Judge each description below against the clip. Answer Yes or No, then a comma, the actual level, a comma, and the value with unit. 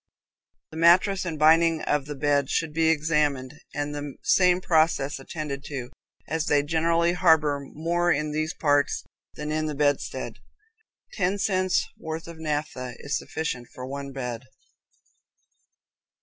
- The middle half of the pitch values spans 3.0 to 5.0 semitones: No, narrow, 2.4 semitones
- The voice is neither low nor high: Yes, medium, 150 Hz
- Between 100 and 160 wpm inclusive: Yes, average, 140 wpm